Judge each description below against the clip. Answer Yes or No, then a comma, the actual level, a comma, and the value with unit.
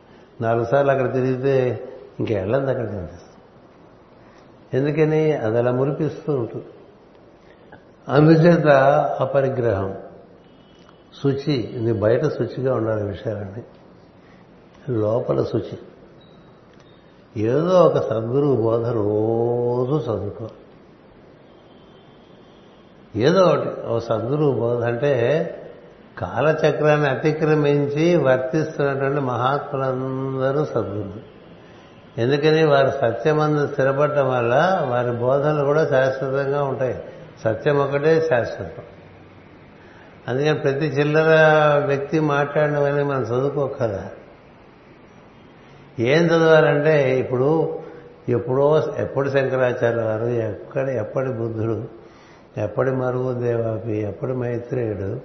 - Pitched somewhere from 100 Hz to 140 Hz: Yes, low, 135 Hz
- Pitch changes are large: No, average, 3.7 semitones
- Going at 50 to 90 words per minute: Yes, average, 85 wpm